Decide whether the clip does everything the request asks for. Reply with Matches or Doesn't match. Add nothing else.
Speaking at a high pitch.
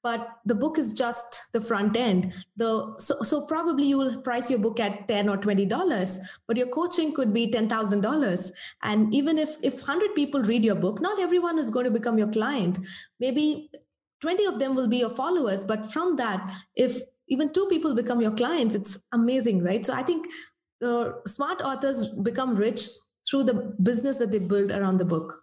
Matches